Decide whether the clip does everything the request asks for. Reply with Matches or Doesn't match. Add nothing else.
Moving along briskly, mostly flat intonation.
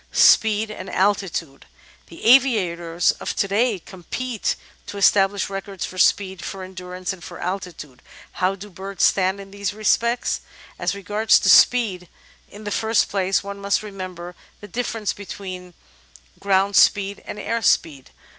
Doesn't match